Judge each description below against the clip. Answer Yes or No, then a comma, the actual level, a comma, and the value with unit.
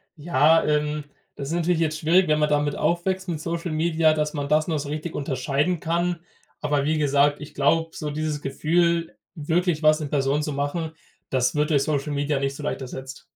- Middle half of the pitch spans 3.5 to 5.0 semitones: No, narrow, 2.4 semitones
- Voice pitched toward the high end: No, medium, 150 Hz